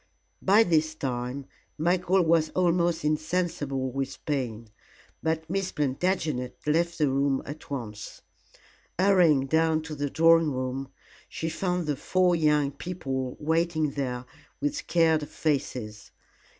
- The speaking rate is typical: No, slow, 125 wpm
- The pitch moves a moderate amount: Yes, average, 3.9 semitones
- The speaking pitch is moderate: Yes, medium, 155 Hz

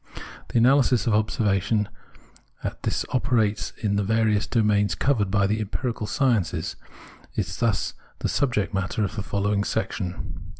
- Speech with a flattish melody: Yes, narrow, 2.2 semitones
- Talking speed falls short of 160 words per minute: Yes, average, 140 wpm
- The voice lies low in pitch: Yes, low, 105 Hz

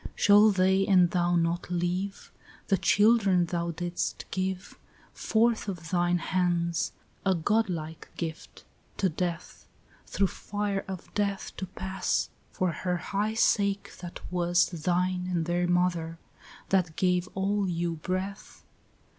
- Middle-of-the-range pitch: Yes, medium, 180 Hz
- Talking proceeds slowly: Yes, slow, 130 wpm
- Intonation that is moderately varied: No, narrow, 2.0 semitones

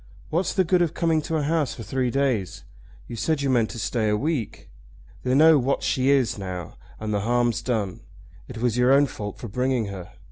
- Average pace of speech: No, fast, 215 wpm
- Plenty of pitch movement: No, average, 4.7 semitones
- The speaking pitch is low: Yes, low, 125 Hz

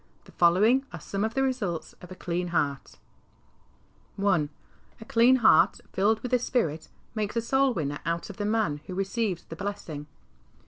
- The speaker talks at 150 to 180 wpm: Yes, average, 175 wpm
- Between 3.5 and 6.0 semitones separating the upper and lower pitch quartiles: Yes, average, 5.3 semitones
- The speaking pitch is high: Yes, high, 195 Hz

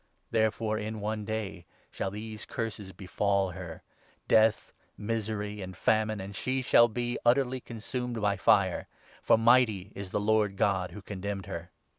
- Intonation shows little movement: Yes, narrow, 2.3 semitones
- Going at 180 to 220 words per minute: No, average, 165 wpm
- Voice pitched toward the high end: No, low, 105 Hz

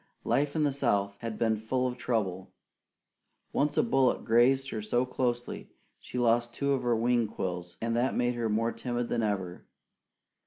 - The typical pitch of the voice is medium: No, low, 120 Hz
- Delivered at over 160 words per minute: Yes, average, 180 wpm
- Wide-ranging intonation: No, narrow, 2.5 semitones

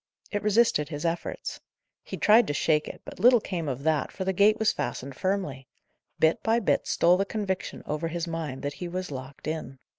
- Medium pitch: Yes, medium, 170 Hz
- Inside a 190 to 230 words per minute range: Yes, fast, 205 wpm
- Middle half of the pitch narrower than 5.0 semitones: No, average, 5.3 semitones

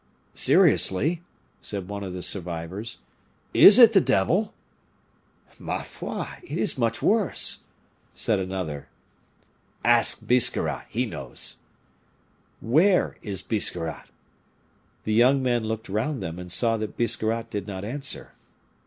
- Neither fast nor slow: No, slow, 120 wpm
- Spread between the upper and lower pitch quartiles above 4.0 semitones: Yes, average, 5.2 semitones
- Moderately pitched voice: No, low, 110 Hz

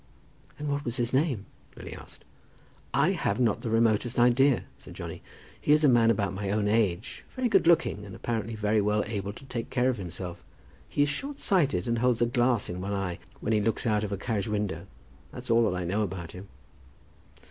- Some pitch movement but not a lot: Yes, average, 3.8 semitones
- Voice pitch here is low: Yes, low, 115 Hz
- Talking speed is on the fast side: Yes, fast, 210 wpm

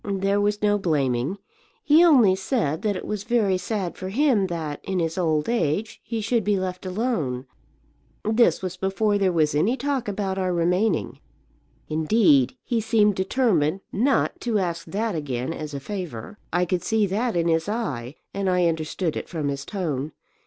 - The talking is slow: No, average, 175 wpm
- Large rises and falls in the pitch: No, average, 4.7 semitones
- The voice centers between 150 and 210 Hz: Yes, high, 190 Hz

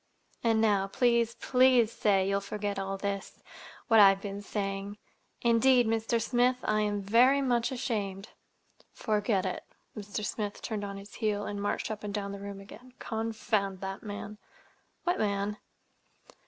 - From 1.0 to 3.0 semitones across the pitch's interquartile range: Yes, narrow, 2.5 semitones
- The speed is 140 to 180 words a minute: Yes, average, 150 wpm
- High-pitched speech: Yes, high, 210 Hz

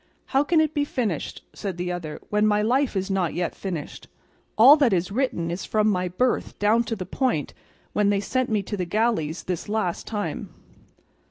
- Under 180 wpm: No, average, 195 wpm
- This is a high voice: Yes, high, 205 Hz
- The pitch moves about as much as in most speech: Yes, average, 4.7 semitones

